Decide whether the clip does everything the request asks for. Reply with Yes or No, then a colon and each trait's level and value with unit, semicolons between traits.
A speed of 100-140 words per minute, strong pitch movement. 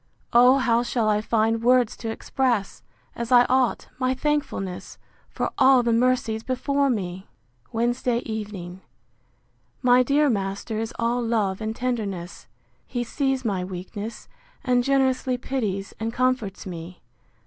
No: slow, 135 wpm; average, 3.4 semitones